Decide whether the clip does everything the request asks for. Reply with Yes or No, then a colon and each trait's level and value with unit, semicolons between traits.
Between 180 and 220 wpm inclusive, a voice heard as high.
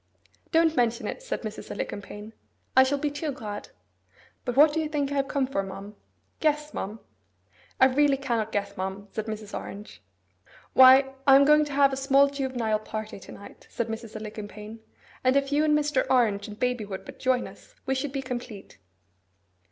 Yes: average, 190 wpm; very high, 255 Hz